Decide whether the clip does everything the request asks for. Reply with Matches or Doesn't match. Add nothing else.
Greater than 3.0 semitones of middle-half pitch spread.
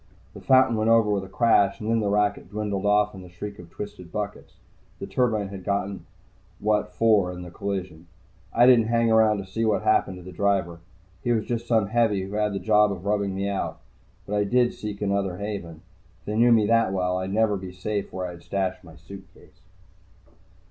Doesn't match